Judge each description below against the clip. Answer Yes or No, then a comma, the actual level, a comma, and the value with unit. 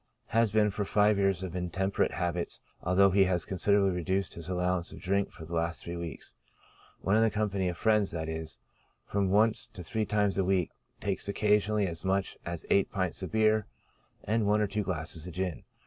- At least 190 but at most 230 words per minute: Yes, average, 195 wpm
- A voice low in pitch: Yes, very low, 95 Hz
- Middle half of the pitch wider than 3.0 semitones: No, average, 2.7 semitones